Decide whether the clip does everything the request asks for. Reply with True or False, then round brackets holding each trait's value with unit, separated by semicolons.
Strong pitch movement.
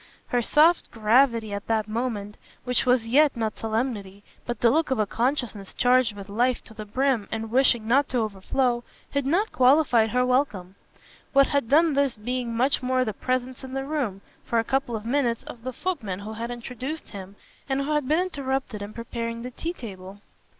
False (3.5 semitones)